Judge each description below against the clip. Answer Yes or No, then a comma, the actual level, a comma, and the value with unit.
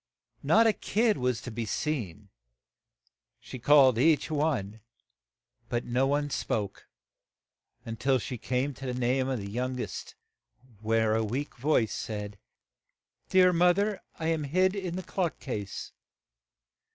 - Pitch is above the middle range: No, low, 130 Hz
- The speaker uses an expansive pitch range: Yes, wide, 5.9 semitones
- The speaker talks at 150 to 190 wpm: No, average, 140 wpm